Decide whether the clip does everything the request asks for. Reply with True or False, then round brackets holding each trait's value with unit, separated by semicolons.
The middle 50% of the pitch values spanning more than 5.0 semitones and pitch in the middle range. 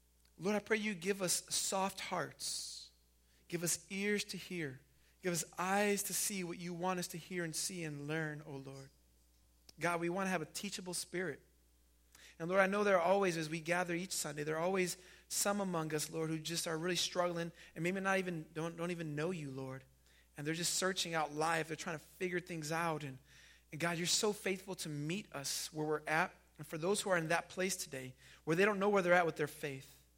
False (3.4 semitones; 170 Hz)